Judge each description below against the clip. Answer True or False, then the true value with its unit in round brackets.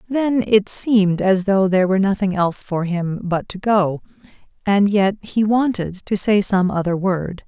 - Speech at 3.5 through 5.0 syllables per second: True (4.6 syllables/s)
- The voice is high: True (195 Hz)